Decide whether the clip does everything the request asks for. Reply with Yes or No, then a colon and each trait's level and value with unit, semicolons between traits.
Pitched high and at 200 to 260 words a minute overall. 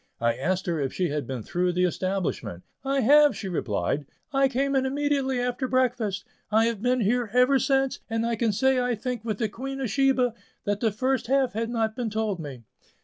Yes: high, 230 Hz; fast, 205 wpm